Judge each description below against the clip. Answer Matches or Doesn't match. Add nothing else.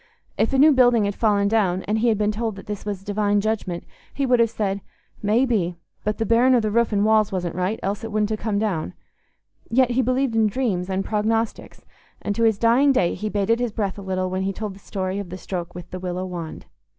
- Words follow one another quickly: Matches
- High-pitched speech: Matches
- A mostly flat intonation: Doesn't match